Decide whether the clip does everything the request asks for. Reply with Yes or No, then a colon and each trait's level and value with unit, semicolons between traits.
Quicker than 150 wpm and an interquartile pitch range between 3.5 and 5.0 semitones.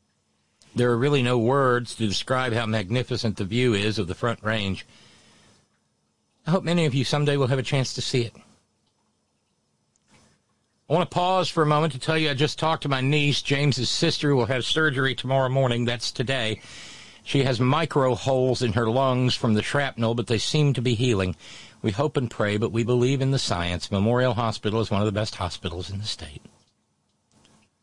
Yes: average, 200 wpm; average, 3.9 semitones